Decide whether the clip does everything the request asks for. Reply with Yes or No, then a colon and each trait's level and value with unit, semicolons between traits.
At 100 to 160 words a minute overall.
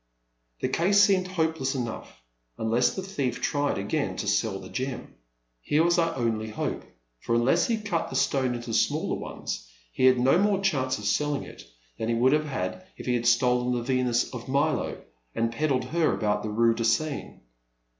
No: average, 195 wpm